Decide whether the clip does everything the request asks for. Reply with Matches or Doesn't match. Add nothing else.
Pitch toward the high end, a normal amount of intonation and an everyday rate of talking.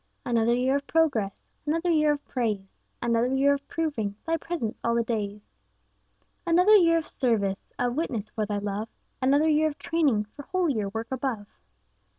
Doesn't match